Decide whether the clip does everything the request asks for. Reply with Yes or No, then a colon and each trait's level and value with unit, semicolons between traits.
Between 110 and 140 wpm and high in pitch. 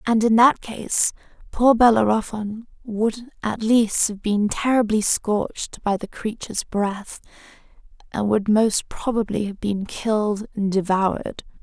Yes: slow, 135 wpm; high, 215 Hz